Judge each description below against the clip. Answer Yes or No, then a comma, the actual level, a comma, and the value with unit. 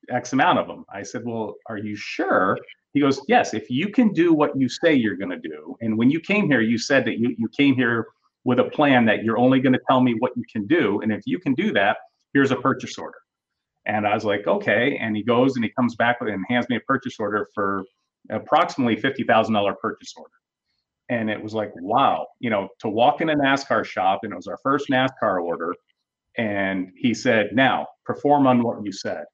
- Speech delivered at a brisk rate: Yes, fast, 230 wpm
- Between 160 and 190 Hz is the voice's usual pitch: No, low, 120 Hz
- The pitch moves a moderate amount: Yes, average, 4.1 semitones